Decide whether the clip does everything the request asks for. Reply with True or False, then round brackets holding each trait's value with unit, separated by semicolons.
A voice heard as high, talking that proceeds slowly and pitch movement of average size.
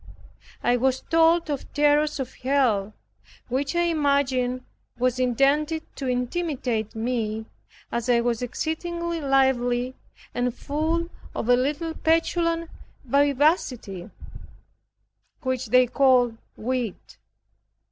True (265 Hz; 105 wpm; 3.8 semitones)